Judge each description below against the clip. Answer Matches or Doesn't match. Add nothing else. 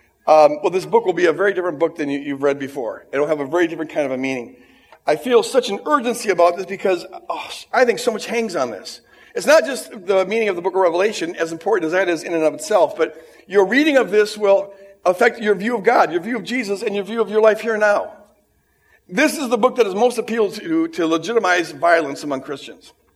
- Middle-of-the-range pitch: Doesn't match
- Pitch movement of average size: Doesn't match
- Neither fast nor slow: Doesn't match